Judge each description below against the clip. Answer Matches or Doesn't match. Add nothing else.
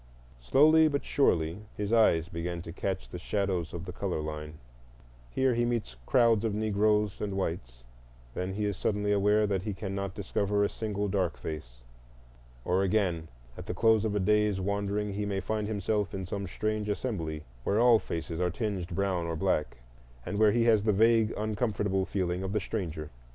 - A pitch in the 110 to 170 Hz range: Doesn't match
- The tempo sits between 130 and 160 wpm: Doesn't match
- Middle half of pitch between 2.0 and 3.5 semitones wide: Matches